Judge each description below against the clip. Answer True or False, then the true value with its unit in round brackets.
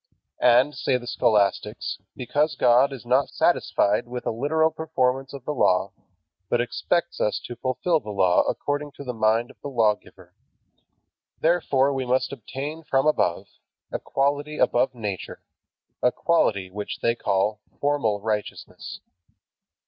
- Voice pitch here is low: True (125 Hz)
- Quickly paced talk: False (140 wpm)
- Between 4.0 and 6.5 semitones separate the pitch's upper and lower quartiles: True (4.5 semitones)